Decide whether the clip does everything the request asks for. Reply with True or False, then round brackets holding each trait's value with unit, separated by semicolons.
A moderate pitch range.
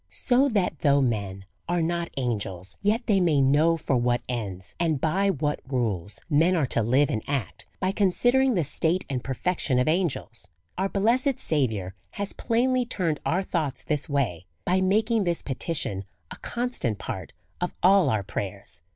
False (7.7 semitones)